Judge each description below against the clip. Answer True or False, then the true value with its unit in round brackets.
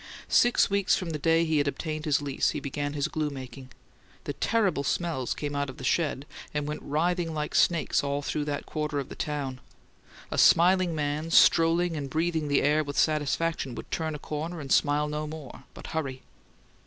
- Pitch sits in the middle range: True (150 Hz)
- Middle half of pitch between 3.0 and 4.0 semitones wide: False (2.4 semitones)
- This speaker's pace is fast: False (195 wpm)